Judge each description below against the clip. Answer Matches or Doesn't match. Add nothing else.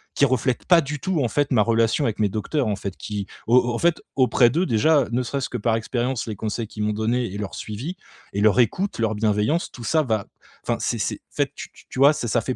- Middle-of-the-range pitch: Doesn't match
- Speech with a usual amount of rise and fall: Matches